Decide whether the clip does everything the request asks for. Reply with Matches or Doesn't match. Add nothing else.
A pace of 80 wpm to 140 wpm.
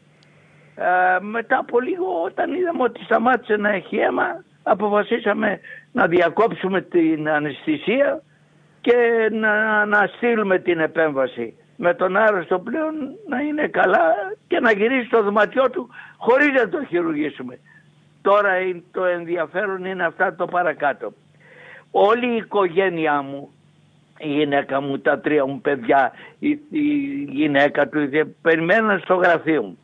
Matches